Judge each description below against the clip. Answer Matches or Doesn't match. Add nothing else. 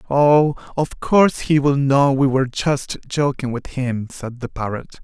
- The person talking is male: Matches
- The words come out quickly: Doesn't match